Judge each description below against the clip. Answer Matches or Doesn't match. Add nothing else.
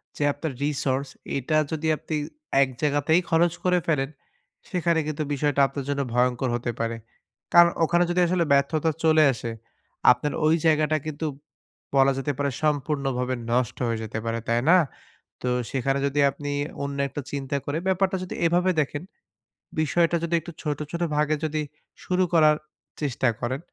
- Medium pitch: Matches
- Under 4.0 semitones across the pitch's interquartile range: Matches